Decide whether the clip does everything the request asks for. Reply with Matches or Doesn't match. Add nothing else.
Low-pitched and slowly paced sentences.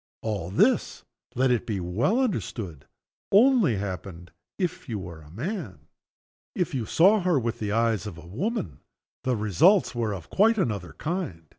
Doesn't match